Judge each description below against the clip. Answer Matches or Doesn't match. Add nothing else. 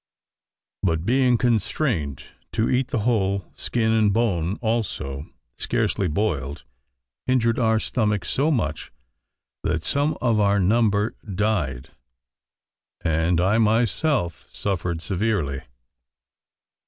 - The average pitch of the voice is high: Doesn't match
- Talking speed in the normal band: Doesn't match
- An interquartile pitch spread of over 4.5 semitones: Matches